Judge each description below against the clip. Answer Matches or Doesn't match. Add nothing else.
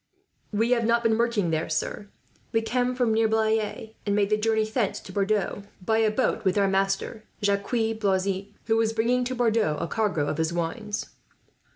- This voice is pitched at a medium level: Doesn't match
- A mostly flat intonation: Matches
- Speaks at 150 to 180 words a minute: Doesn't match